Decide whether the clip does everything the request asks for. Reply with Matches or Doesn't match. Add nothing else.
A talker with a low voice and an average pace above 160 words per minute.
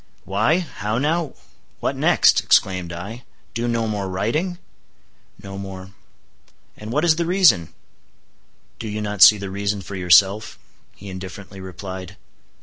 Doesn't match